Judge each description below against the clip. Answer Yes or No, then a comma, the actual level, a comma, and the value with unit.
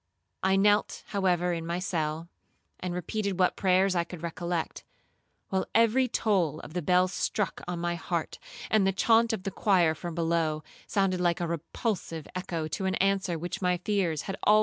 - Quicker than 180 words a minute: Yes, average, 190 wpm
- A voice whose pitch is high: No, medium, 180 Hz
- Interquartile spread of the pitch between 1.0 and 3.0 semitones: Yes, narrow, 2.5 semitones